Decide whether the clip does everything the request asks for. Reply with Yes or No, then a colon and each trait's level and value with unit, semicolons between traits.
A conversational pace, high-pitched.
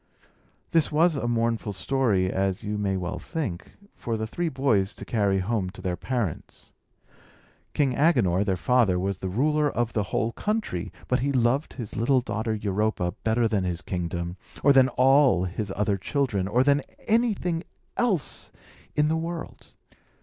No: average, 165 wpm; low, 115 Hz